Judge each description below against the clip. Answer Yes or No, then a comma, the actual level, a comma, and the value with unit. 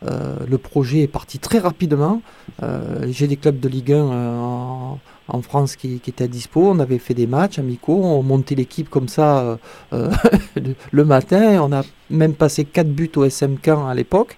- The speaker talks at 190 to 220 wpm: Yes, average, 195 wpm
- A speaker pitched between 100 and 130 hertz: No, medium, 140 Hz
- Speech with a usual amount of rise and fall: Yes, average, 3.3 semitones